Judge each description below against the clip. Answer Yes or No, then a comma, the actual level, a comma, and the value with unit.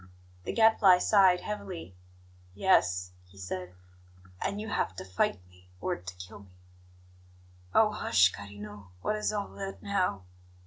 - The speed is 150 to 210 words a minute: No, average, 140 wpm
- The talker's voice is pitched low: Yes, low, 100 Hz